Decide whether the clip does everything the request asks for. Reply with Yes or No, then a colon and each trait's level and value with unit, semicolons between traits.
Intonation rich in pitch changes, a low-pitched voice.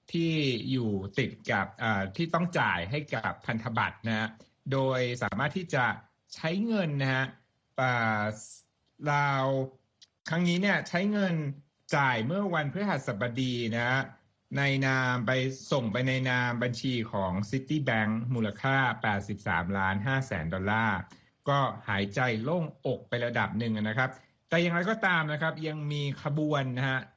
No: average, 4.9 semitones; low, 130 Hz